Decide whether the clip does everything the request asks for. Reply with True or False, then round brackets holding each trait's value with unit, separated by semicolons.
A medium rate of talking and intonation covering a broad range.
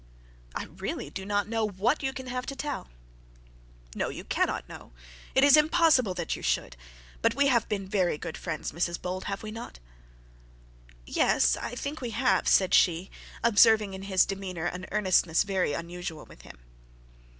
False (170 wpm; 5.0 semitones)